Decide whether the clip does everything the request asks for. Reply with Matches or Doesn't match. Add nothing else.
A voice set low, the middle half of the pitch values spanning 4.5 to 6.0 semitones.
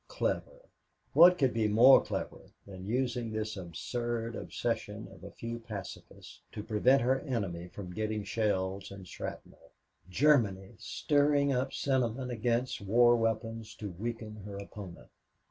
Doesn't match